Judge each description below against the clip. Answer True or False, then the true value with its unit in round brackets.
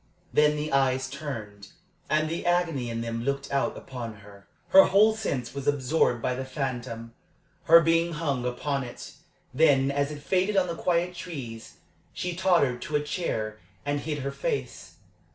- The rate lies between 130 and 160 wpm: False (170 wpm)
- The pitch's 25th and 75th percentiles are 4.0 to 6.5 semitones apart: True (5.0 semitones)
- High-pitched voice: False (140 Hz)